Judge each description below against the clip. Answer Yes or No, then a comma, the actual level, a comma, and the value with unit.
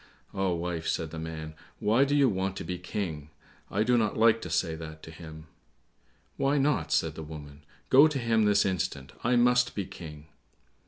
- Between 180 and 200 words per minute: Yes, average, 195 wpm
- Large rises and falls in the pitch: Yes, wide, 6.3 semitones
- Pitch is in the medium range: No, very low, 95 Hz